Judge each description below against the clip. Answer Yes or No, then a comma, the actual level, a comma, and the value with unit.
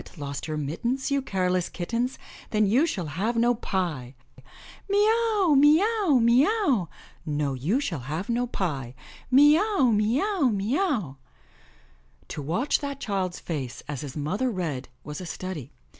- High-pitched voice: Yes, high, 205 Hz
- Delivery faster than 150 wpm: Yes, average, 160 wpm